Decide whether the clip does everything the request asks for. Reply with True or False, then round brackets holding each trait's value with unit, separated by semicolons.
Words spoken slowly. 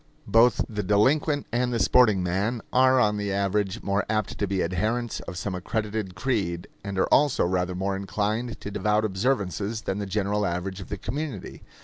False (185 wpm)